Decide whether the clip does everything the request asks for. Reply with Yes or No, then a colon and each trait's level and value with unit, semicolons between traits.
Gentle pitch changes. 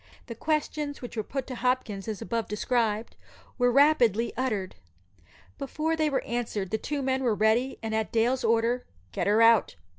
No: average, 3.2 semitones